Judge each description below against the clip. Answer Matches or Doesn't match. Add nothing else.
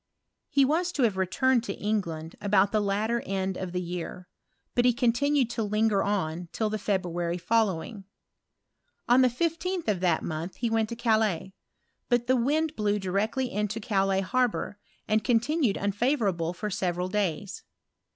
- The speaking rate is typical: Matches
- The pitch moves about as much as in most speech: Matches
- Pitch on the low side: Doesn't match